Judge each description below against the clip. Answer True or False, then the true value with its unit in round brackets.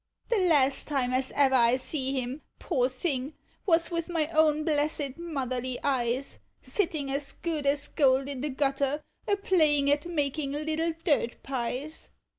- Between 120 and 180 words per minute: True (155 wpm)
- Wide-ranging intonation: False (3.0 semitones)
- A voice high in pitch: True (285 Hz)